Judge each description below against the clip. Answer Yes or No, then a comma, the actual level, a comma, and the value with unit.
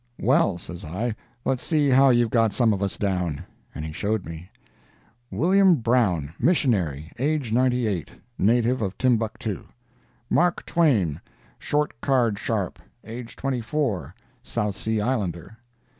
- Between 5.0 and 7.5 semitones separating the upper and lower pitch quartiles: Yes, wide, 5.4 semitones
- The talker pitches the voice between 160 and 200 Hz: No, low, 110 Hz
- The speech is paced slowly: Yes, slow, 105 wpm